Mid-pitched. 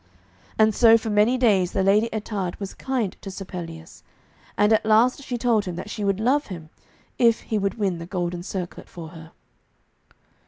No: high, 205 Hz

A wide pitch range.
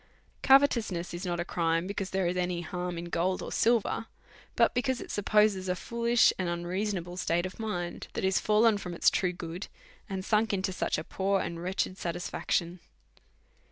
No: average, 3.3 semitones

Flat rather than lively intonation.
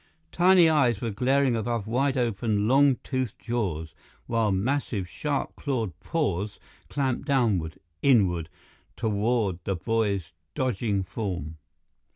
No: average, 5.1 semitones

